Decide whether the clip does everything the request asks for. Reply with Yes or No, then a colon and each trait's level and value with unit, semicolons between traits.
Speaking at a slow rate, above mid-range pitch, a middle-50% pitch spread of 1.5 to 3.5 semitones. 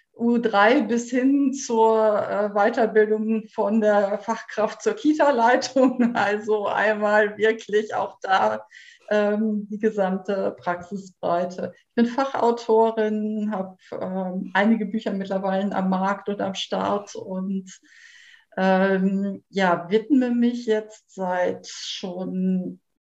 Yes: slow, 105 wpm; high, 215 Hz; average, 3.1 semitones